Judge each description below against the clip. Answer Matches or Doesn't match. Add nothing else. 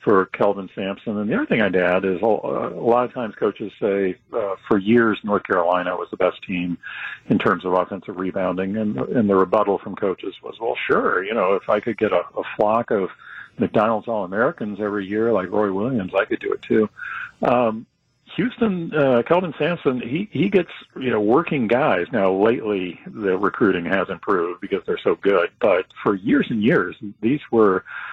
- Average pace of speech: Matches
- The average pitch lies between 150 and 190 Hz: Doesn't match